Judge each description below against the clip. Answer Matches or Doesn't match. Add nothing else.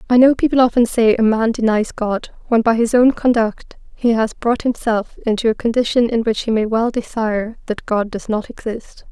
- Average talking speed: Doesn't match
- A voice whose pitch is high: Matches